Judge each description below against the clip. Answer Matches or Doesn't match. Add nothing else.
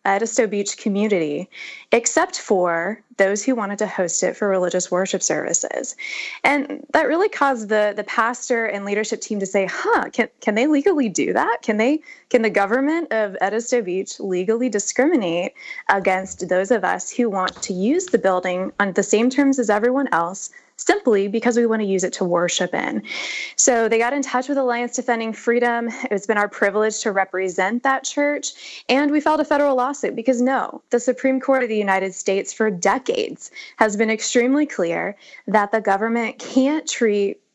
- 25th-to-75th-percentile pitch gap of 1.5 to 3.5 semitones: Doesn't match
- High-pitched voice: Matches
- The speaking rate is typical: Matches